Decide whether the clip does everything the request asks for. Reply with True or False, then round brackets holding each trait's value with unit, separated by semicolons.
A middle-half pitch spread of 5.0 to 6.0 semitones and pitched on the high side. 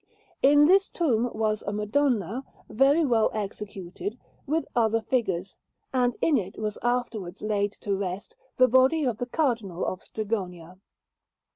False (4.2 semitones; 220 Hz)